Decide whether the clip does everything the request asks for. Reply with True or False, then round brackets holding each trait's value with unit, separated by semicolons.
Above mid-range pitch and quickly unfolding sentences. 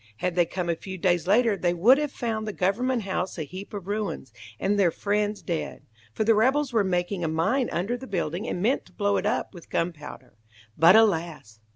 True (195 Hz; 215 wpm)